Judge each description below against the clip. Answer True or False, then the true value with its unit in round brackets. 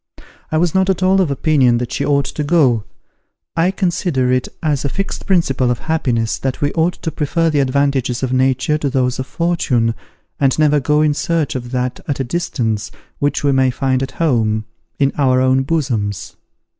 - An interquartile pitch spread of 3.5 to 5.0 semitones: True (3.8 semitones)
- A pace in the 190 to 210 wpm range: True (195 wpm)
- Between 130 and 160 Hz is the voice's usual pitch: True (140 Hz)